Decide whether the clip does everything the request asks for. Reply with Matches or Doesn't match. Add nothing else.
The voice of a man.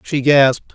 Matches